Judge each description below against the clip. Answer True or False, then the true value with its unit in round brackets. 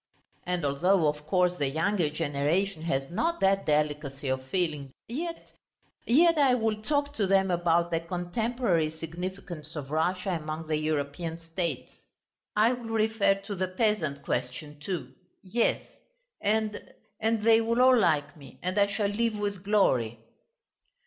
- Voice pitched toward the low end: False (180 Hz)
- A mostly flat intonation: False (5.6 semitones)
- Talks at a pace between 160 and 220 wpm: False (150 wpm)